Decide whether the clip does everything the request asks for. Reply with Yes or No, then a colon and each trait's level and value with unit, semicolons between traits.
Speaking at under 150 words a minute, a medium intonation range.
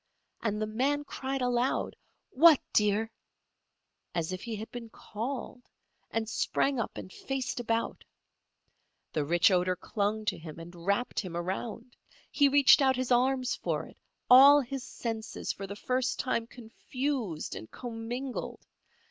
Yes: average, 140 wpm; average, 4.2 semitones